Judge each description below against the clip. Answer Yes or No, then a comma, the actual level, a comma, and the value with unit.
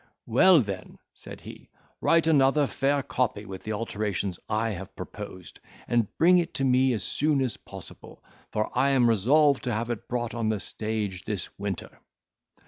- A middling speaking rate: Yes, average, 170 wpm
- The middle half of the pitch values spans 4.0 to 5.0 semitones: Yes, average, 4.6 semitones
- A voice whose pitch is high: No, low, 115 Hz